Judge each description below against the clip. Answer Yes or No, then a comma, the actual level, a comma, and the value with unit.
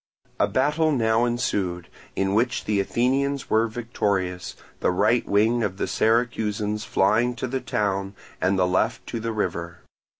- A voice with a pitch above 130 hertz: No, low, 110 Hz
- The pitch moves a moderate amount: Yes, average, 3.7 semitones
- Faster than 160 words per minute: No, average, 155 wpm